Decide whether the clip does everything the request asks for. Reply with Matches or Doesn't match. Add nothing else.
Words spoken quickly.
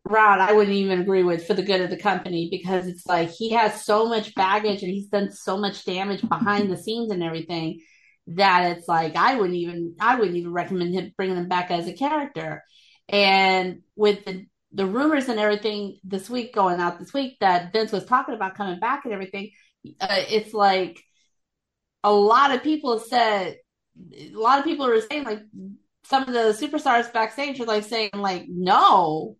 Doesn't match